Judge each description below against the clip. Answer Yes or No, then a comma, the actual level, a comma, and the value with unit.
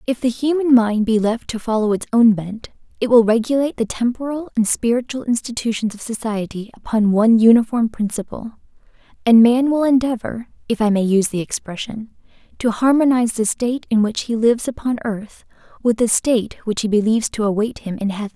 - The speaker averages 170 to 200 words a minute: Yes, average, 185 wpm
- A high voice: Yes, high, 230 Hz